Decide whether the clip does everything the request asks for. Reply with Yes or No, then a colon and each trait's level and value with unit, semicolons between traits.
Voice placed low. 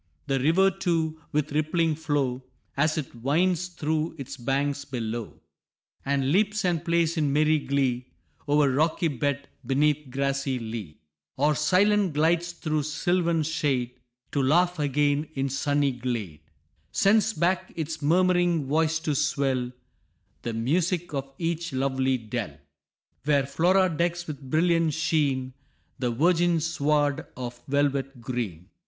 No: medium, 150 Hz